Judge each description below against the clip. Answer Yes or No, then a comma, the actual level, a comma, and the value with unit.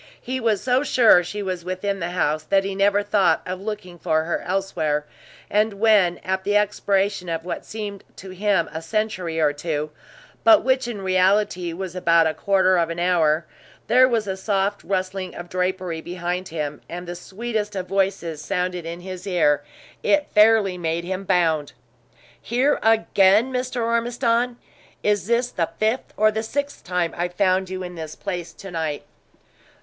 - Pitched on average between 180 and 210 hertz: Yes, high, 190 Hz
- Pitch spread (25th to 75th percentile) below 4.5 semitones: Yes, average, 3.3 semitones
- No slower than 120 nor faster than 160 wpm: No, average, 170 wpm